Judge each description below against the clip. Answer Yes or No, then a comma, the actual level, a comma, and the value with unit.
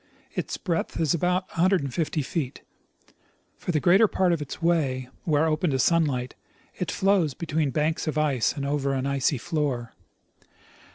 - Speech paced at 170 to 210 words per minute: No, average, 155 wpm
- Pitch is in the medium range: Yes, medium, 155 Hz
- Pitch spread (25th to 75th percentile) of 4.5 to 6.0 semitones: No, average, 3.6 semitones